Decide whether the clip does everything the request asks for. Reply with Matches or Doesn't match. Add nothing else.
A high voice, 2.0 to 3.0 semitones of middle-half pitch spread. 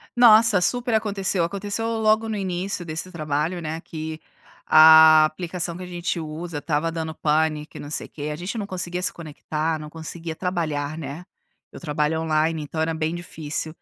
Doesn't match